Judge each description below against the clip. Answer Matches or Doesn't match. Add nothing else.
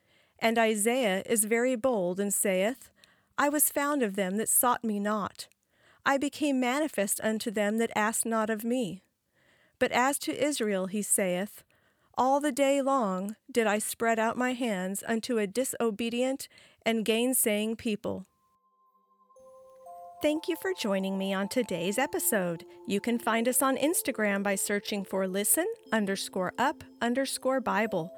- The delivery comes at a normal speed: Matches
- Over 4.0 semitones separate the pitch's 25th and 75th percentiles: Matches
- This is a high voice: Matches